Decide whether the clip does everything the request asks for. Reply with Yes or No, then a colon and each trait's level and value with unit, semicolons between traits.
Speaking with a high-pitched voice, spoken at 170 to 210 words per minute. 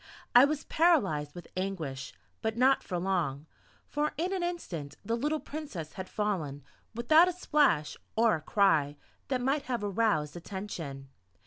No: high, 205 Hz; average, 150 wpm